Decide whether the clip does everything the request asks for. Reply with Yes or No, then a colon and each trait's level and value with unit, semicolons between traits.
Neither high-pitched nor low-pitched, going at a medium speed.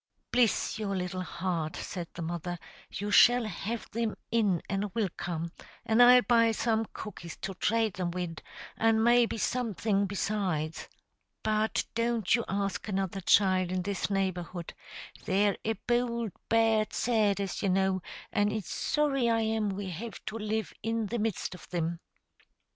No: high, 205 Hz; average, 155 wpm